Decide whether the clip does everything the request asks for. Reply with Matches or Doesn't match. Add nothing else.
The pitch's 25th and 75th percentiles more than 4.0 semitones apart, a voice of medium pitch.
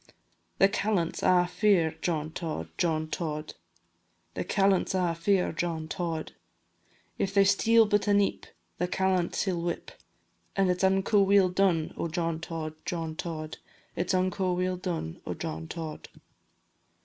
Doesn't match